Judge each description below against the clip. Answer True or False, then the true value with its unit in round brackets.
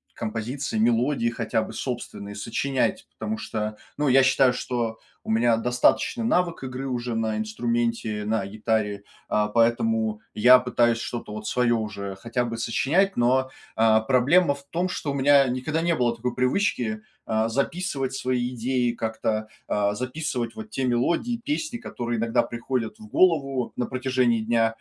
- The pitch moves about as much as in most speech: True (3.0 semitones)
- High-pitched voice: False (120 Hz)